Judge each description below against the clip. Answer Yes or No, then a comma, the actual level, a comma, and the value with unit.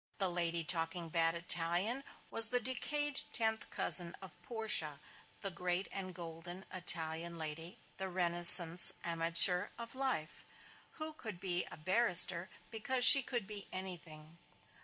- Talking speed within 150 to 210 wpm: No, slow, 135 wpm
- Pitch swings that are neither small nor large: Yes, average, 4.7 semitones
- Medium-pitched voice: Yes, medium, 180 Hz